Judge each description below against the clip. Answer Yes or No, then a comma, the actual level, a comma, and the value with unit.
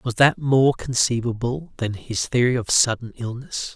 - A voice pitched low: Yes, low, 125 Hz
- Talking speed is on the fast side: No, average, 160 wpm